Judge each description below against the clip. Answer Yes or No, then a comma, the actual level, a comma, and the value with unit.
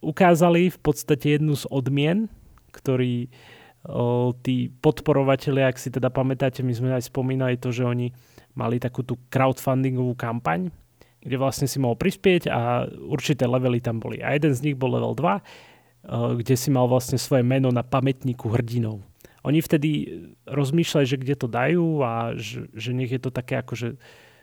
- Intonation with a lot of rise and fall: No, average, 2.7 semitones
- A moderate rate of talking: No, fast, 170 wpm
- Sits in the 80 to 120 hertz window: No, low, 130 Hz